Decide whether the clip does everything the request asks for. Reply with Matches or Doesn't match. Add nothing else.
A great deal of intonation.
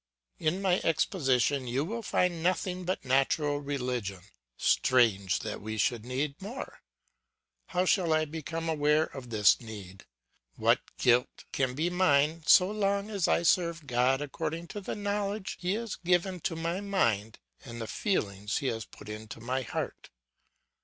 Matches